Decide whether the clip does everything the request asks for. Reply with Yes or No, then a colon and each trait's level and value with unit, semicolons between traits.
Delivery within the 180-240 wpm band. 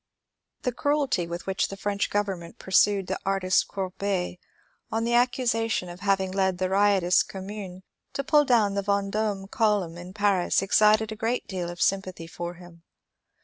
No: average, 165 wpm